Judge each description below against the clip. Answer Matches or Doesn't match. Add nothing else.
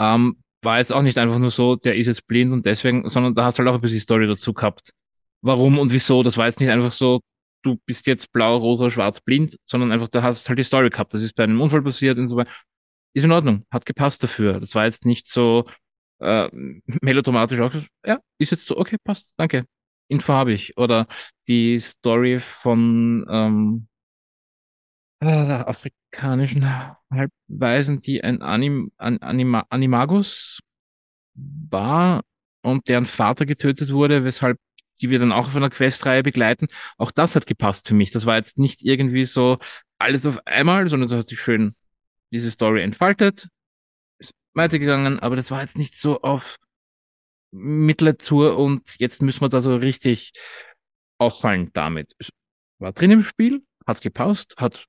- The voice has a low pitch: Matches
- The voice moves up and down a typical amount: Matches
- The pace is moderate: Matches